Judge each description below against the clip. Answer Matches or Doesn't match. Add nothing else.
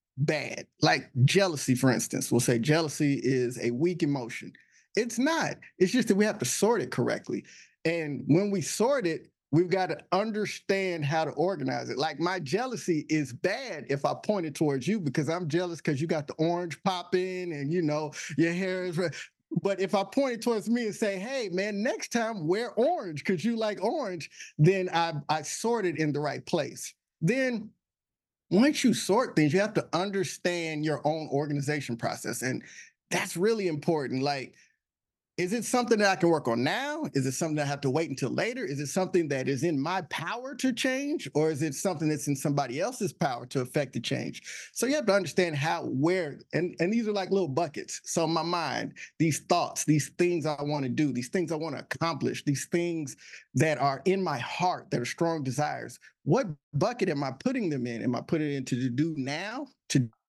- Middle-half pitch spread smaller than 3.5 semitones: Doesn't match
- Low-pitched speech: Doesn't match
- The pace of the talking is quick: Matches